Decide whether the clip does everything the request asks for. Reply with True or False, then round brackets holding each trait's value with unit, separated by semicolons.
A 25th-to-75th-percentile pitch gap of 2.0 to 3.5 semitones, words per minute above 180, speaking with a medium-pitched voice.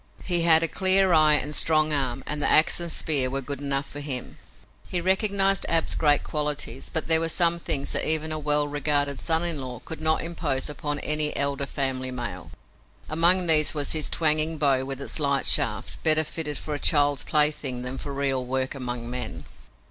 True (2.7 semitones; 200 wpm; 150 Hz)